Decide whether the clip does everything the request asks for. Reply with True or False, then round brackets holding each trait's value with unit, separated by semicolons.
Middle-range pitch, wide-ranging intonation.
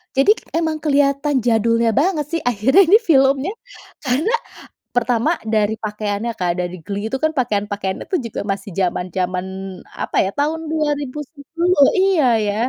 False (255 Hz; 6.7 semitones)